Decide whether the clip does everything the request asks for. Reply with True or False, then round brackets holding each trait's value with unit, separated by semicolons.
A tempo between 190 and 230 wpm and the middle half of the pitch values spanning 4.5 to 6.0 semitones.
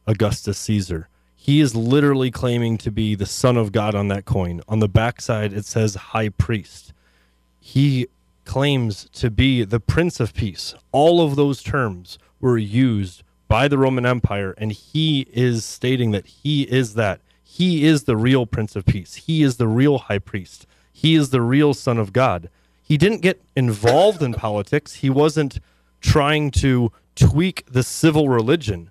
False (170 wpm; 5.0 semitones)